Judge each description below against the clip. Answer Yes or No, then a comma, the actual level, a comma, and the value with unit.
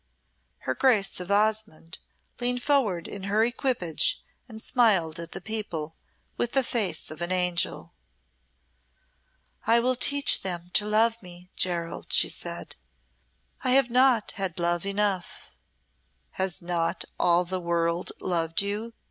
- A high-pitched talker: Yes, high, 195 Hz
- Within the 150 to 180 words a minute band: No, slow, 135 wpm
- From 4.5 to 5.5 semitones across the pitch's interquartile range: Yes, average, 4.8 semitones